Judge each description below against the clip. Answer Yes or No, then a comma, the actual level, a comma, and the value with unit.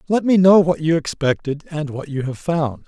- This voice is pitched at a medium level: Yes, medium, 155 Hz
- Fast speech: Yes, fast, 230 wpm